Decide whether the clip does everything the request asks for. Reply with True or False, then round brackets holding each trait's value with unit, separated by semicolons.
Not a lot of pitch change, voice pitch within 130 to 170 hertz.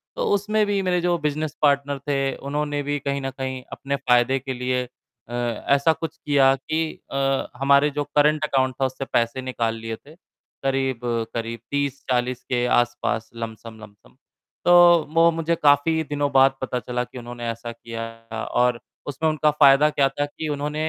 False (3.3 semitones; 135 Hz)